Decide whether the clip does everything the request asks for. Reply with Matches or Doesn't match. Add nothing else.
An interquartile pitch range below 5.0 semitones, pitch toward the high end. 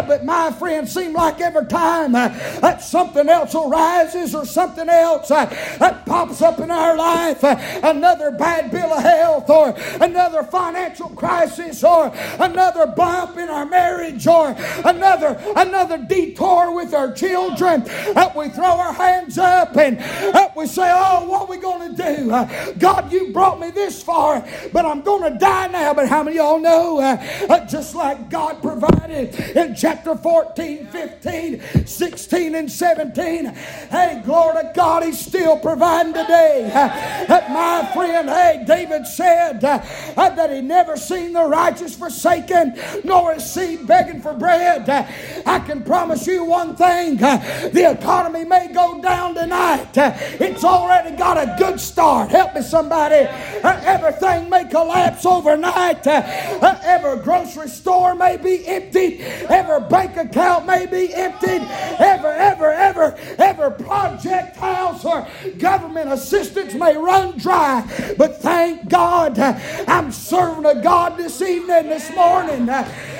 Matches